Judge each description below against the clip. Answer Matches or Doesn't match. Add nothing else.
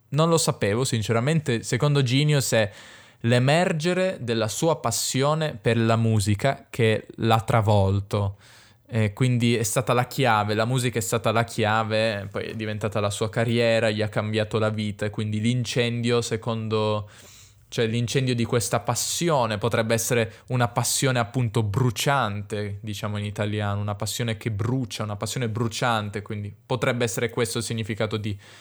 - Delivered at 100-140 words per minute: Doesn't match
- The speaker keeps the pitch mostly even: Matches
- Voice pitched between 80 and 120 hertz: Matches